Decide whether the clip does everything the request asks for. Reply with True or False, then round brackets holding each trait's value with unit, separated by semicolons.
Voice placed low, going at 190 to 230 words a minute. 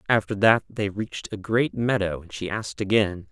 True (105 Hz; 200 wpm)